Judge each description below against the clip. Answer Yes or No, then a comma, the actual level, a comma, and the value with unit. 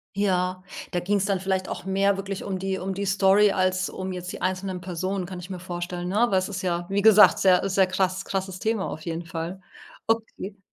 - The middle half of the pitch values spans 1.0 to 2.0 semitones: Yes, narrow, 1.3 semitones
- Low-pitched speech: No, high, 190 Hz